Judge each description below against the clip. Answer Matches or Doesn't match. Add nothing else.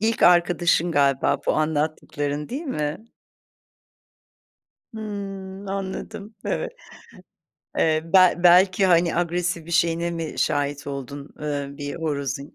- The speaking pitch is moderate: Matches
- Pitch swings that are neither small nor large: Matches